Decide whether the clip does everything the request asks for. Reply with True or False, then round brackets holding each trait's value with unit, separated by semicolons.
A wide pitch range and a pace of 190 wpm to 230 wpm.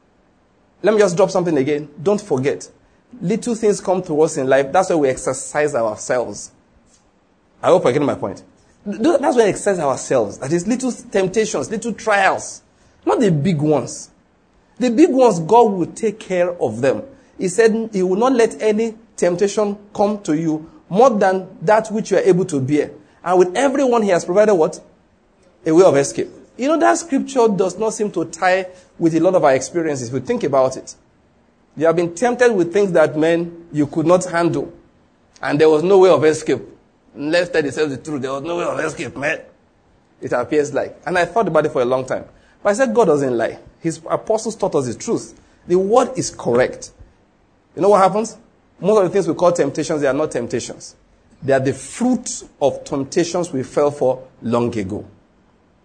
True (5.9 semitones; 200 wpm)